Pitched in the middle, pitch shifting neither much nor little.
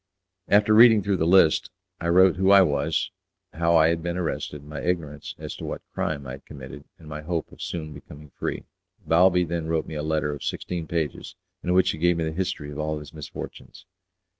No: very low, 80 Hz; average, 3.0 semitones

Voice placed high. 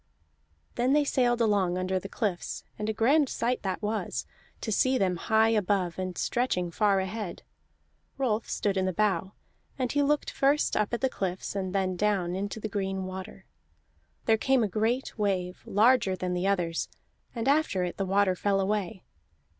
Yes: high, 205 Hz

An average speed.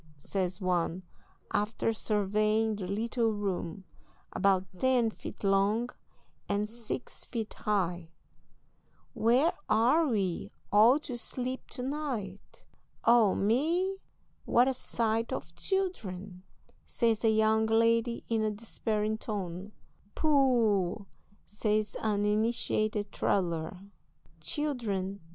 No: slow, 105 wpm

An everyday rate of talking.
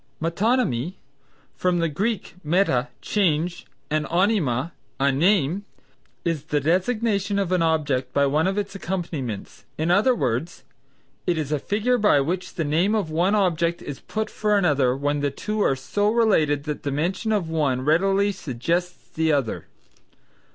Yes: average, 160 wpm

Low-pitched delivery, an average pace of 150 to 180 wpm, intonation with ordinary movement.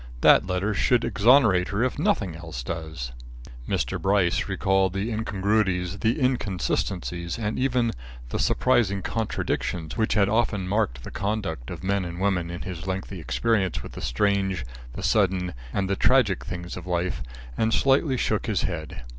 Yes: very low, 95 Hz; average, 160 wpm; average, 3.8 semitones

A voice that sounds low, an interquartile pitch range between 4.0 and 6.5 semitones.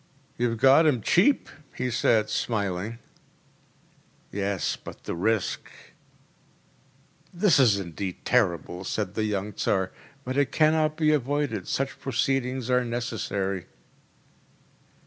Yes: low, 120 Hz; average, 5.3 semitones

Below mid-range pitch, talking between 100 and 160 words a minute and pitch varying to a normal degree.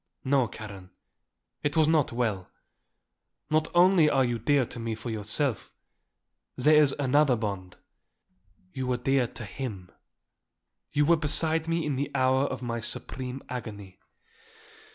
Yes: low, 130 Hz; average, 140 wpm; average, 4.7 semitones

